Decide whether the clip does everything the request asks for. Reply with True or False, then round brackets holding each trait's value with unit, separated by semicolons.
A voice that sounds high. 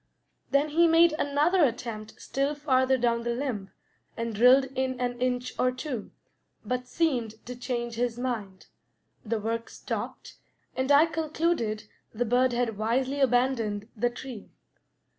True (250 Hz)